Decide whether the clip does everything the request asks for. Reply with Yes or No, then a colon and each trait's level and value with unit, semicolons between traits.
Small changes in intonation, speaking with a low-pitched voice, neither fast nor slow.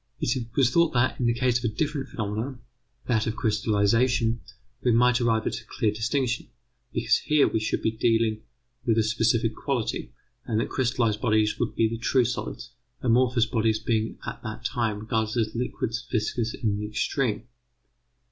Yes: narrow, 2.1 semitones; low, 115 Hz; average, 175 wpm